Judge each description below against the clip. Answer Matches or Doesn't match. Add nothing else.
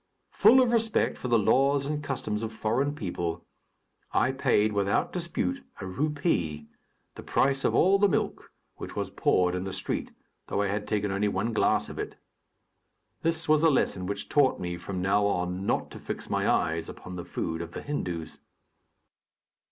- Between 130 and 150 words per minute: Doesn't match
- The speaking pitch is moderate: Doesn't match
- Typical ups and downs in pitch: Doesn't match